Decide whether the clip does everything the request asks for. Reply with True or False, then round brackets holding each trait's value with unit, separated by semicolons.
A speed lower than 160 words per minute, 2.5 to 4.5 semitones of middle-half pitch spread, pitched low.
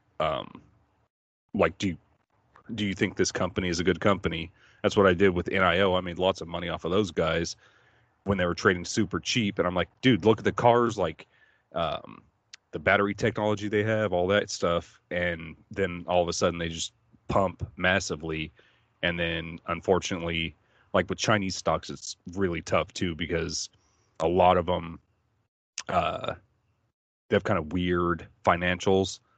False (175 wpm; 3.7 semitones; 90 Hz)